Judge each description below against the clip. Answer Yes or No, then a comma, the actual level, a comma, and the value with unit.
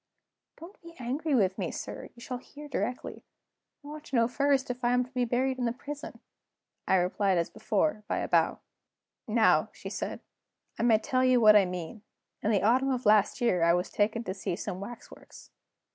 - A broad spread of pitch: No, average, 4.0 semitones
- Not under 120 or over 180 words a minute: No, fast, 205 wpm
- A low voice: No, high, 240 Hz